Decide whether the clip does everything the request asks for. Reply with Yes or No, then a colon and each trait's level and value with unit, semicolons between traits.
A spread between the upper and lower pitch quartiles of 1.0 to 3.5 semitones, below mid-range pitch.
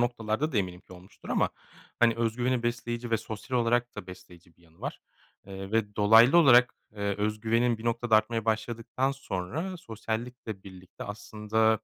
Yes: average, 2.8 semitones; low, 110 Hz